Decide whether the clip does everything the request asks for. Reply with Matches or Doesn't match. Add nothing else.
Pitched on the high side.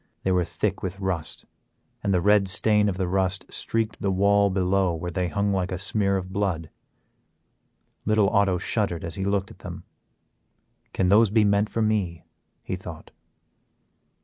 Doesn't match